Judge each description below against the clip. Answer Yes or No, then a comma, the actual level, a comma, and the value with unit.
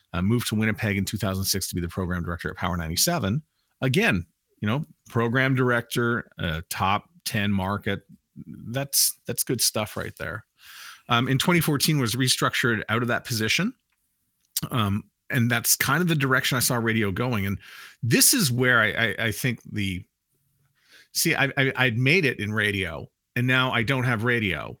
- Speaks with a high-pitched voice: No, low, 120 Hz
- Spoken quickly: No, average, 175 wpm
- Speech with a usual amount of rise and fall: Yes, average, 4.6 semitones